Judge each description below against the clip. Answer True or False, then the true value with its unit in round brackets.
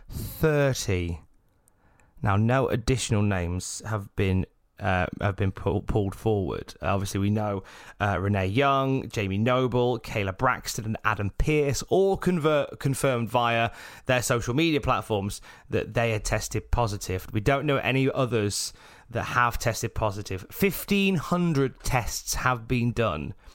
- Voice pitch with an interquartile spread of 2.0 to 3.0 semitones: False (4.7 semitones)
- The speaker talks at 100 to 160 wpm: True (140 wpm)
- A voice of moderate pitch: False (110 Hz)